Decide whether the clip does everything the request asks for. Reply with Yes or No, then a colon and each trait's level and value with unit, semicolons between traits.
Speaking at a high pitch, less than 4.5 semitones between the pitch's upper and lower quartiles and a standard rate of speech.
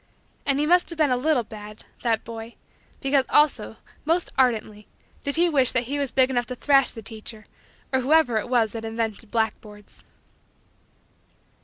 Yes: high, 245 Hz; average, 4.1 semitones; average, 170 wpm